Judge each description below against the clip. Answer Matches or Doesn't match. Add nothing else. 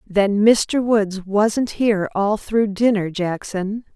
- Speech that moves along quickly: Doesn't match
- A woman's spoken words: Matches